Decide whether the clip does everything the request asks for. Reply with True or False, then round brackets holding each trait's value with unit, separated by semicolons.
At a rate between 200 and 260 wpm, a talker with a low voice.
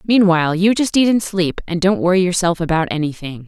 False (205 wpm; 180 Hz)